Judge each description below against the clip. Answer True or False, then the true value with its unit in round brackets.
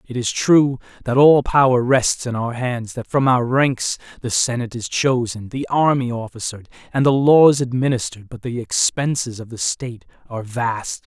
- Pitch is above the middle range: False (125 Hz)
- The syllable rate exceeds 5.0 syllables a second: False (4.9 syllables/s)